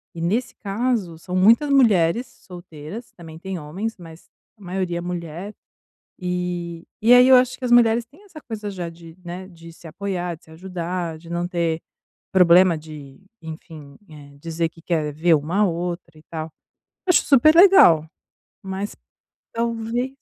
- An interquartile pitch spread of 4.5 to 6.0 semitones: Yes, average, 5.2 semitones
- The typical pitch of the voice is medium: Yes, medium, 180 Hz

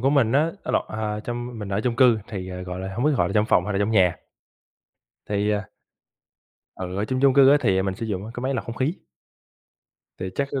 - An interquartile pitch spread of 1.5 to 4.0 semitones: No, average, 4.8 semitones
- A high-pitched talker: No, low, 110 Hz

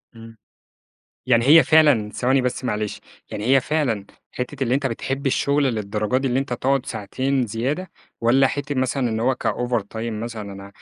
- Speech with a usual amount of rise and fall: Yes, average, 3.2 semitones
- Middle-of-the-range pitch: No, low, 125 Hz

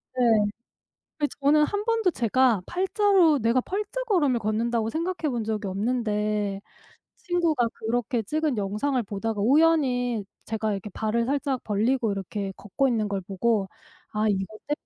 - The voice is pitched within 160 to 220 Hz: No, high, 235 Hz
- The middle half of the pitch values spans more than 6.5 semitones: No, wide, 5.6 semitones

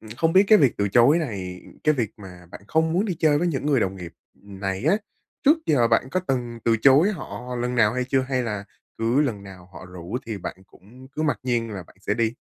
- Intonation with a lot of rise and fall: Yes, wide, 6.3 semitones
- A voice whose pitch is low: Yes, low, 120 Hz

